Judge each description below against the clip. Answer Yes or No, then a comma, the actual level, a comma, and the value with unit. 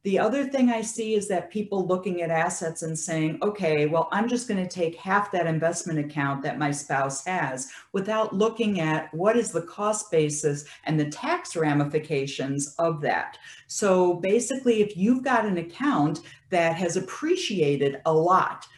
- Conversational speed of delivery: Yes, average, 175 wpm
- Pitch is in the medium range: Yes, medium, 175 Hz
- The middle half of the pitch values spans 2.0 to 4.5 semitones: No, wide, 5.4 semitones